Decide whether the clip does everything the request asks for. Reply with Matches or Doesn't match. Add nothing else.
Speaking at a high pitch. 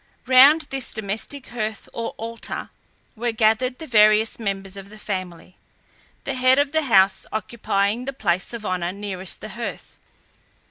Matches